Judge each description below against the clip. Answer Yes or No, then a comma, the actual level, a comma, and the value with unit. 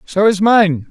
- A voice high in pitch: Yes, high, 195 Hz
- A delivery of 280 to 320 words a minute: No, average, 200 wpm